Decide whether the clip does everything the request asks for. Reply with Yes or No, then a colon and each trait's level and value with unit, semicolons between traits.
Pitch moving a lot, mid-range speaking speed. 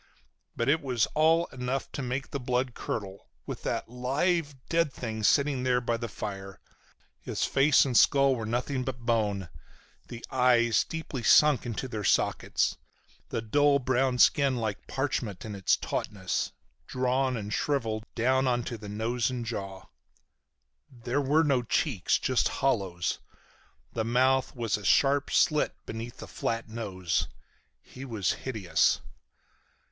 No: average, 3.4 semitones; average, 145 wpm